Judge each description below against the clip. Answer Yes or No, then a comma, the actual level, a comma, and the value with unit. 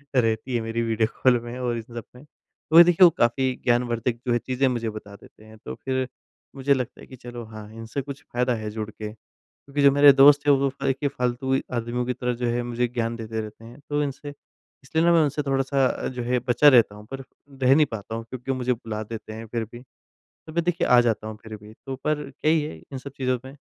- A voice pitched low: Yes, low, 125 Hz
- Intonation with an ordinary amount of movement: Yes, average, 3.1 semitones